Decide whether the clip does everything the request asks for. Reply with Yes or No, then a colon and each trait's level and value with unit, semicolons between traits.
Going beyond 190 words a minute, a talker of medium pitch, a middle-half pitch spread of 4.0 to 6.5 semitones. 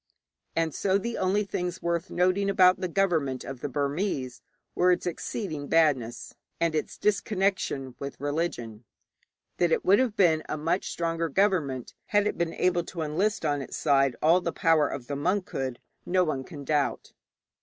No: average, 165 wpm; medium, 165 Hz; average, 4.5 semitones